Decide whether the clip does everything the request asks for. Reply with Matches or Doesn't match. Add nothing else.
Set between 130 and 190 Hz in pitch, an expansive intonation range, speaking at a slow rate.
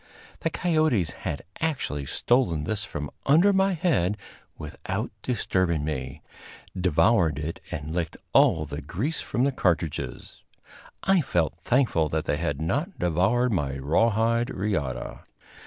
Doesn't match